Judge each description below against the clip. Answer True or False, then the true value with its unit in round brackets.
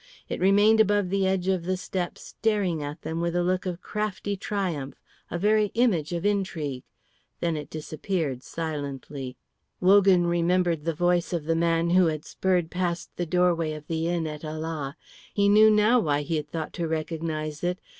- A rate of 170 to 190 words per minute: True (180 wpm)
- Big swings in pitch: False (3.3 semitones)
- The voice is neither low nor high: True (170 Hz)